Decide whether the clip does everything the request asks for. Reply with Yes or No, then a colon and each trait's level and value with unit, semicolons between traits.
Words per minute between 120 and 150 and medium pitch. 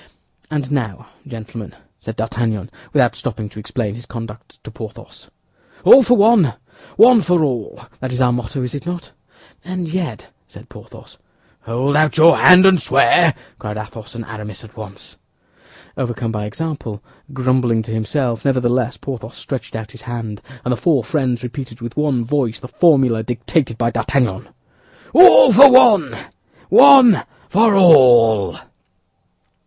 No: average, 145 wpm; low, 125 Hz